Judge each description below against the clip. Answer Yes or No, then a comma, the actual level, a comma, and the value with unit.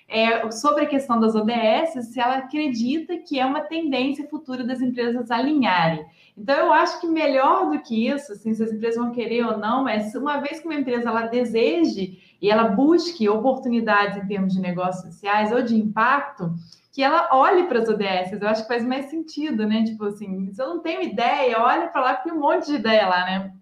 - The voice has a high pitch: Yes, high, 240 Hz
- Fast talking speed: Yes, fast, 215 wpm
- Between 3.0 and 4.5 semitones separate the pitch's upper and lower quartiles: No, average, 5.2 semitones